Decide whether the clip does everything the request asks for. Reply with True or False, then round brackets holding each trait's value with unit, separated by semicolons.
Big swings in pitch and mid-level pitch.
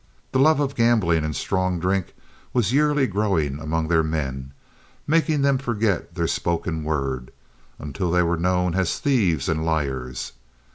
False (6.8 semitones; 90 Hz)